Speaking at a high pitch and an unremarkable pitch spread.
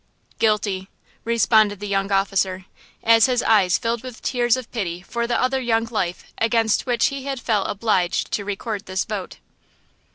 Yes: high, 220 Hz; average, 3.2 semitones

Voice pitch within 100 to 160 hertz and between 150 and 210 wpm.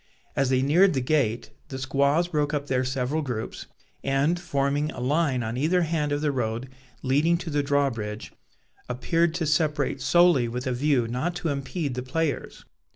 Yes: medium, 140 Hz; average, 175 wpm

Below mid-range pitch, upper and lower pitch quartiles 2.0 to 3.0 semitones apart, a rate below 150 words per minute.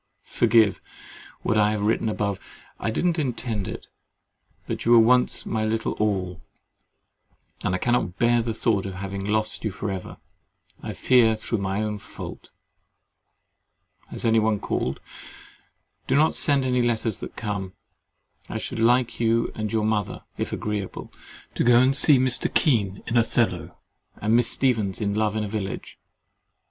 No: low, 110 Hz; average, 2.7 semitones; average, 160 wpm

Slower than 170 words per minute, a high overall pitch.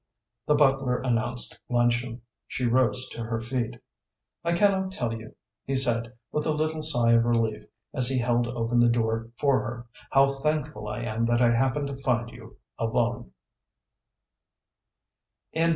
No: average, 150 wpm; low, 120 Hz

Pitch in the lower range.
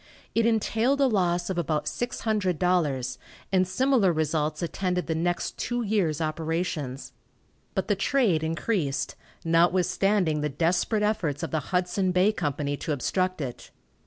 No: medium, 180 Hz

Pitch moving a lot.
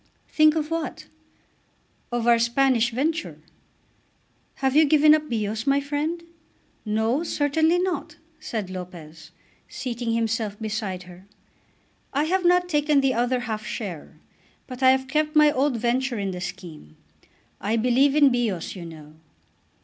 Yes: wide, 5.7 semitones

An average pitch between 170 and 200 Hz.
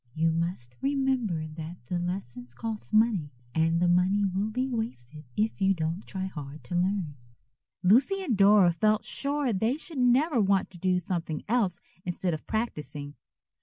Yes: high, 190 Hz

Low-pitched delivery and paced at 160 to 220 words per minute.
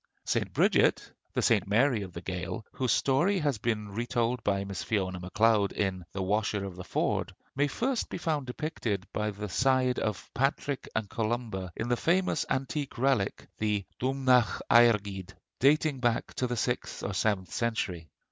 Yes: low, 110 Hz; average, 165 wpm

